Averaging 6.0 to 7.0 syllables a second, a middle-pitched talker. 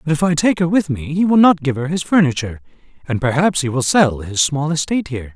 Yes: 6.3 syllables/s; medium, 150 Hz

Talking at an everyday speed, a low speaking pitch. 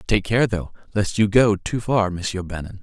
No: fast, 215 wpm; low, 100 Hz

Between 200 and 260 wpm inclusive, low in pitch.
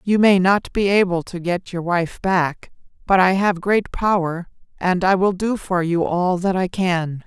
No: fast, 205 wpm; medium, 185 Hz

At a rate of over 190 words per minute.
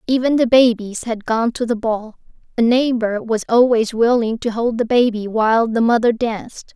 No: average, 185 wpm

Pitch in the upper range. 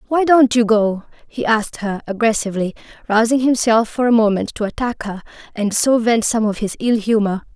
Yes: high, 225 Hz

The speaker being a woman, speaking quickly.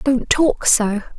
No: female; average, 150 wpm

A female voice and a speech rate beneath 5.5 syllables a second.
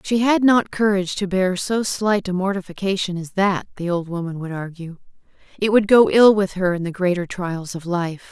Yes: female; 5.2 syllables/s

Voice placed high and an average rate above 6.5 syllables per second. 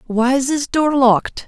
No: very high, 260 Hz; 4.6 syllables/s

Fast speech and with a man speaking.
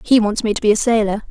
No: fast, 320 wpm; female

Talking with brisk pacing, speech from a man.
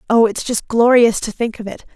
No: fast, 245 wpm; female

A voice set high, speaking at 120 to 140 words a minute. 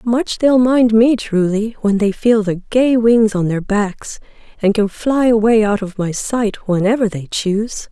No: high, 215 Hz; average, 190 wpm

